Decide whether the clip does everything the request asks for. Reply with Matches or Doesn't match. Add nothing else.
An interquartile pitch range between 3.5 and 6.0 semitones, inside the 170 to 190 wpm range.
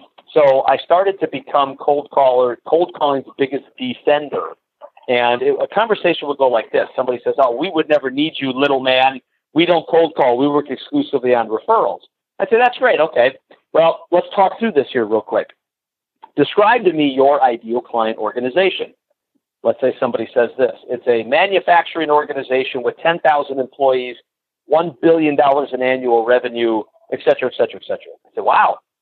Matches